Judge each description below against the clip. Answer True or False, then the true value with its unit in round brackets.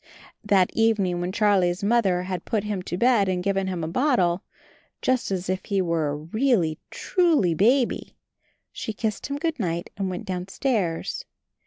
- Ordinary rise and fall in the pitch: True (4.1 semitones)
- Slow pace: False (165 wpm)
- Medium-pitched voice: False (195 Hz)